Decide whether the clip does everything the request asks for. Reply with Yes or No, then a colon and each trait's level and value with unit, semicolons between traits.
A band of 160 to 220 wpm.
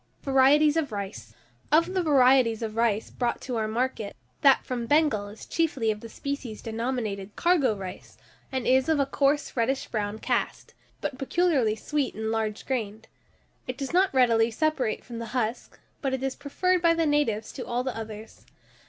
Yes: average, 180 wpm